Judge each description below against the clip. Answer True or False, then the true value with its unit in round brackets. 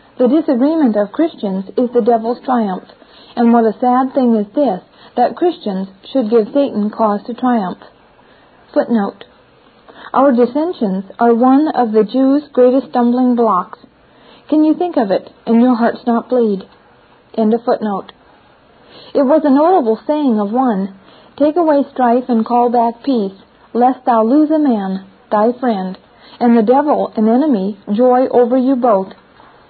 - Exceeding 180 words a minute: False (155 wpm)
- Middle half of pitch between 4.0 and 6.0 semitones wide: False (3.3 semitones)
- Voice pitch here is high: True (245 Hz)